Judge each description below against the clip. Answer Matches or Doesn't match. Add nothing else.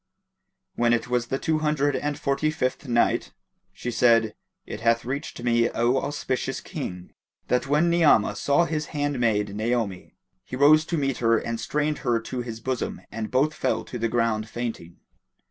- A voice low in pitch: Matches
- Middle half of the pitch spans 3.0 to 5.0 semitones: Matches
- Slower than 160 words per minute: Doesn't match